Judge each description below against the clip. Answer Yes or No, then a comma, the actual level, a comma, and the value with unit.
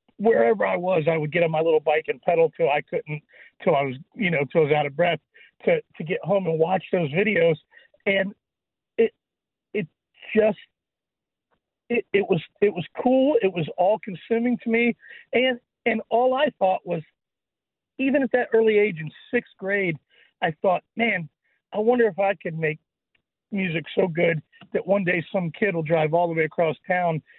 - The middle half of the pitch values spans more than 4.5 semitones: Yes, wide, 5.6 semitones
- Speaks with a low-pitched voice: No, high, 190 Hz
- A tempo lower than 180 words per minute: No, average, 195 wpm